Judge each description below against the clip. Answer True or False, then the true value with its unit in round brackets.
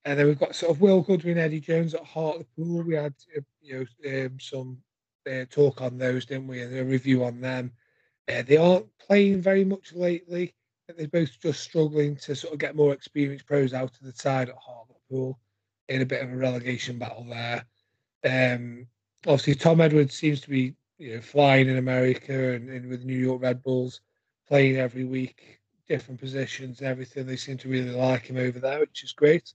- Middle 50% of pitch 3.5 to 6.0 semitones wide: False (2.8 semitones)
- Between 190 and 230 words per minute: True (200 wpm)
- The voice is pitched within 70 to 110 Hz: False (130 Hz)